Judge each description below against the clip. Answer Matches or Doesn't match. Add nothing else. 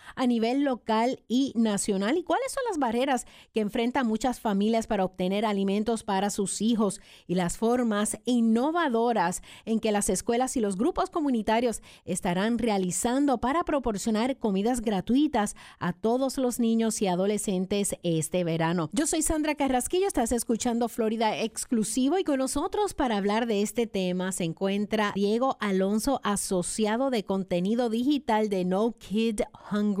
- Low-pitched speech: Doesn't match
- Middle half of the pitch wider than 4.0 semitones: Doesn't match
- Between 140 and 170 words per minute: Matches